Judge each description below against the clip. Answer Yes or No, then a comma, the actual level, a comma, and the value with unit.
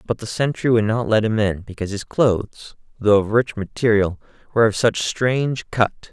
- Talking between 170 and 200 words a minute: Yes, average, 195 wpm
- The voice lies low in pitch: Yes, low, 110 Hz